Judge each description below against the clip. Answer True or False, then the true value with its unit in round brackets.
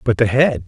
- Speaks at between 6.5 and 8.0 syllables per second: False (5.3 syllables/s)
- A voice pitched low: True (115 Hz)